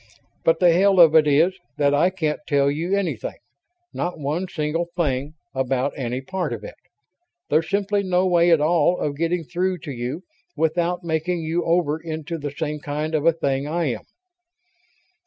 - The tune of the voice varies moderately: Yes, average, 3.2 semitones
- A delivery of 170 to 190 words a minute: Yes, average, 175 wpm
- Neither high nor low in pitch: Yes, medium, 160 Hz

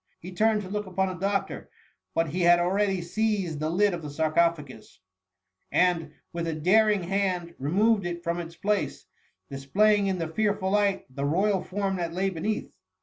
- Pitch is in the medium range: Yes, medium, 180 Hz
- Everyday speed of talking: Yes, average, 175 wpm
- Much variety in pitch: No, average, 3.2 semitones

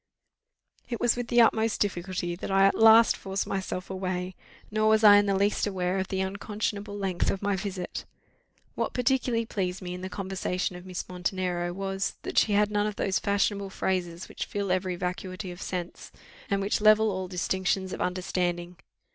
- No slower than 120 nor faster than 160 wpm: No, average, 185 wpm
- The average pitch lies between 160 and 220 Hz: Yes, high, 190 Hz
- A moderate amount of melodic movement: No, narrow, 2.1 semitones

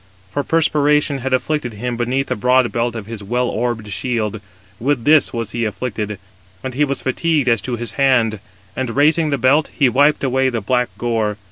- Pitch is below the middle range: Yes, low, 125 Hz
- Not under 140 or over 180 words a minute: No, average, 195 wpm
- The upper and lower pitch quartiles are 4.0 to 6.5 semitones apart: No, average, 3.3 semitones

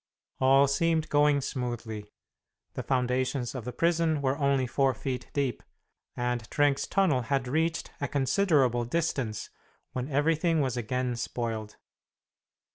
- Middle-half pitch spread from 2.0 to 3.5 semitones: Yes, average, 3.2 semitones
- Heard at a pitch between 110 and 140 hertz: Yes, low, 135 Hz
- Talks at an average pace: No, slow, 125 wpm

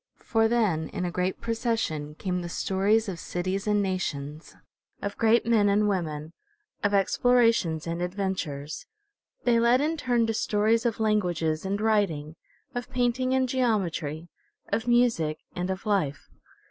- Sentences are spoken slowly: No, average, 145 wpm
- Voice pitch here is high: Yes, high, 200 Hz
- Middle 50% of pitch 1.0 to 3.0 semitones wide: No, average, 5.1 semitones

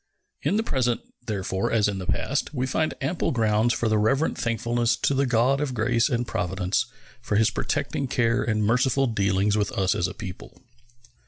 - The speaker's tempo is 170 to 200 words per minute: Yes, average, 180 wpm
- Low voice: Yes, low, 115 Hz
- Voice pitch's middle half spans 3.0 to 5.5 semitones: Yes, average, 3.6 semitones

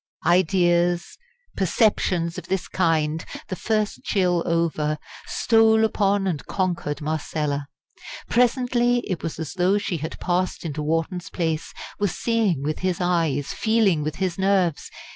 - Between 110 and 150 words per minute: Yes, slow, 135 wpm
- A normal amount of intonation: Yes, average, 3.7 semitones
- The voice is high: No, medium, 175 Hz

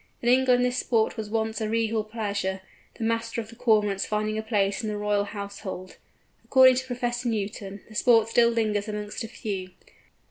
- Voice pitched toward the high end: Yes, high, 220 Hz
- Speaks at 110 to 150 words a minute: No, average, 185 wpm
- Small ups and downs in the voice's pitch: Yes, narrow, 2.1 semitones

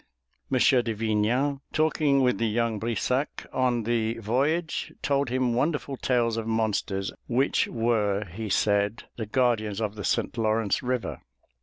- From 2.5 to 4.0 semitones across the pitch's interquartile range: Yes, average, 3.1 semitones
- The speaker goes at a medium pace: Yes, average, 145 wpm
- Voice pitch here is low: Yes, low, 115 Hz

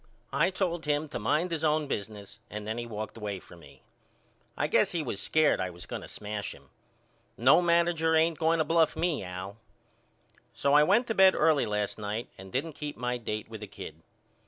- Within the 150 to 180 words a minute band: No, fast, 205 wpm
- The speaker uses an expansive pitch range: Yes, wide, 7.5 semitones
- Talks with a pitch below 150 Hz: Yes, medium, 140 Hz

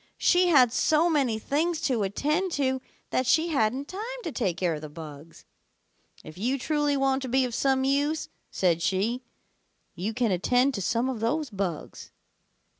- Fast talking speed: No, average, 175 wpm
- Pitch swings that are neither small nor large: No, wide, 6.3 semitones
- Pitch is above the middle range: Yes, very high, 255 Hz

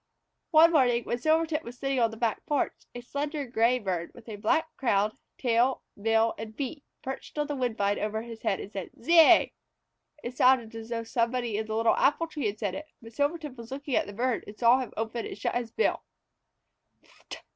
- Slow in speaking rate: No, average, 200 wpm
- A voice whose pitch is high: Yes, high, 240 Hz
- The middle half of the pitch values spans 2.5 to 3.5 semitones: No, average, 3.9 semitones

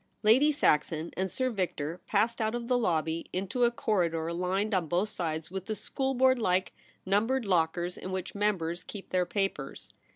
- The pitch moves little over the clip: No, average, 4.4 semitones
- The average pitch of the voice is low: No, high, 190 Hz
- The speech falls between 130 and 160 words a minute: No, average, 170 wpm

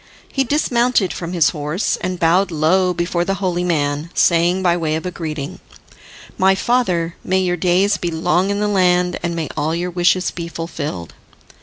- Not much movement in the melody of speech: Yes, narrow, 2.3 semitones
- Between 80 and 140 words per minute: No, average, 175 wpm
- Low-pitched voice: No, medium, 175 Hz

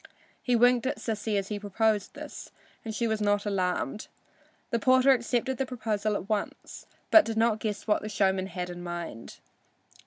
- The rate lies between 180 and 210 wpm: Yes, average, 185 wpm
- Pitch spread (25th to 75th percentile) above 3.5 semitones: No, average, 2.9 semitones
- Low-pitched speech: No, high, 215 Hz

